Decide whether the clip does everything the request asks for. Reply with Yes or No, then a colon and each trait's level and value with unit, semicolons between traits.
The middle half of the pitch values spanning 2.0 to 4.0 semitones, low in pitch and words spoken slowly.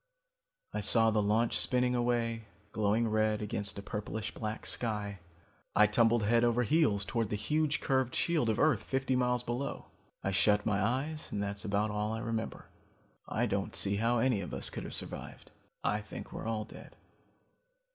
No: average, 2.8 semitones; low, 110 Hz; average, 175 wpm